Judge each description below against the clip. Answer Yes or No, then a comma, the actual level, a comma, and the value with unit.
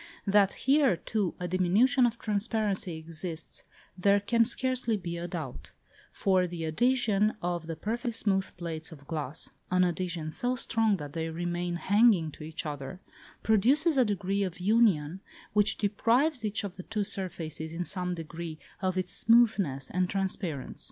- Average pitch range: Yes, average, 4.7 semitones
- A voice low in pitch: No, medium, 185 Hz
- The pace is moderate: Yes, average, 160 wpm